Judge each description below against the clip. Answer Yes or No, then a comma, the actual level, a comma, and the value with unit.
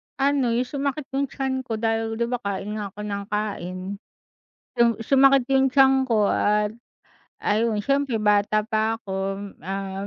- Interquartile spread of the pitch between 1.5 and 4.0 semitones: No, average, 4.4 semitones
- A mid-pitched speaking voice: No, high, 225 Hz